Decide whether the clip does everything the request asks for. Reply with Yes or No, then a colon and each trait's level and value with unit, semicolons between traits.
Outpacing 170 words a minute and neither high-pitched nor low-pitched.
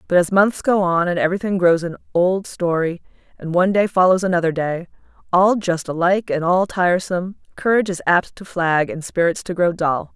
Yes: average, 195 wpm; medium, 180 Hz